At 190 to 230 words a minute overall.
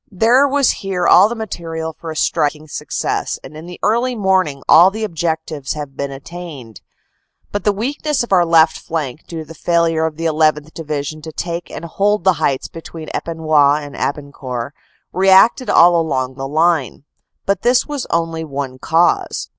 No: average, 175 wpm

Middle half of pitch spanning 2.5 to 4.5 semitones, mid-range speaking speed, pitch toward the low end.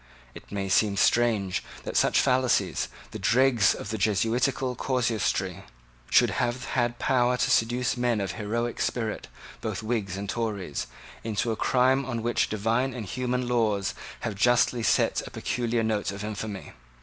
Yes: average, 2.8 semitones; average, 155 wpm; low, 115 Hz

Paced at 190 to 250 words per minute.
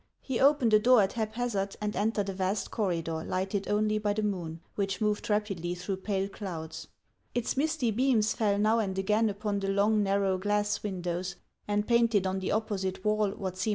Yes: average, 195 wpm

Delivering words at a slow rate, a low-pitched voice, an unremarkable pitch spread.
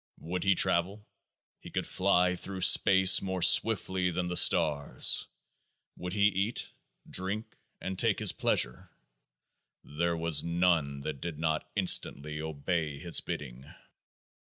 Yes: slow, 130 wpm; very low, 90 Hz; average, 3.3 semitones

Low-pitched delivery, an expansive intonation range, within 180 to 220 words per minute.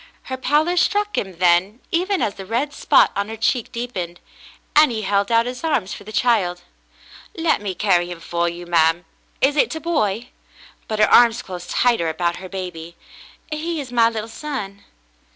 No: high, 215 Hz; wide, 6.8 semitones; average, 185 wpm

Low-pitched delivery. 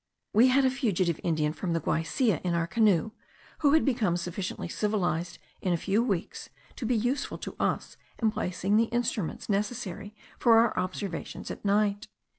No: high, 205 Hz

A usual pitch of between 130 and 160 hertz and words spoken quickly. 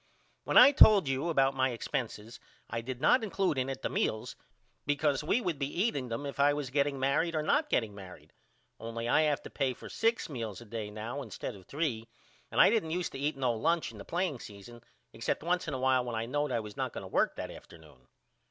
Yes: low, 135 Hz; fast, 235 wpm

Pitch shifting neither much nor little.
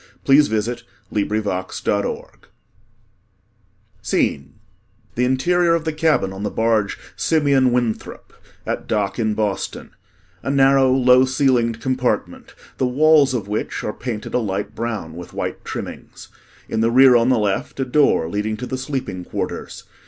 Yes: average, 4.0 semitones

